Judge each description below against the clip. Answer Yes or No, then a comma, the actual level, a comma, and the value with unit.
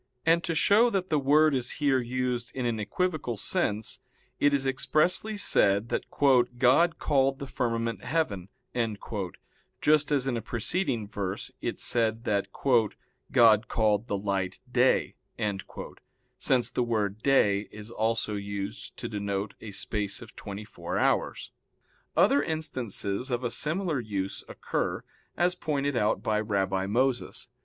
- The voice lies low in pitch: Yes, low, 120 Hz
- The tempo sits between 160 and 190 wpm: No, average, 140 wpm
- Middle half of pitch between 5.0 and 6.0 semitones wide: Yes, average, 5.3 semitones